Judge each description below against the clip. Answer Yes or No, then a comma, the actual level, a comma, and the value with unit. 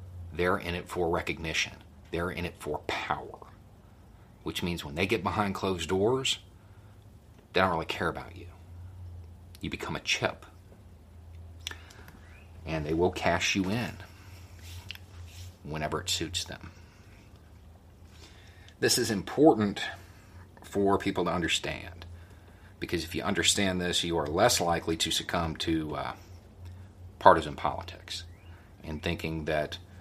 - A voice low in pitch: Yes, very low, 90 Hz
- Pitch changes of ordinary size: No, narrow, 2.1 semitones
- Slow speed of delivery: Yes, slow, 125 wpm